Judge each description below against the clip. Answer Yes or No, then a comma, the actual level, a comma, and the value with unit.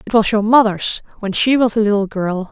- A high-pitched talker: Yes, high, 210 Hz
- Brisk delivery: Yes, fast, 240 wpm